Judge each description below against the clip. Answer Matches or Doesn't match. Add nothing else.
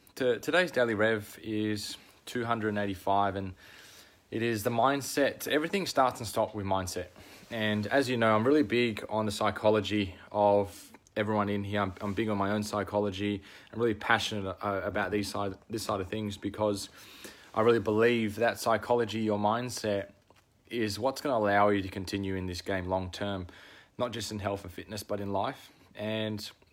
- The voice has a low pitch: Matches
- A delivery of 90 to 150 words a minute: Doesn't match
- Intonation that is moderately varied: Doesn't match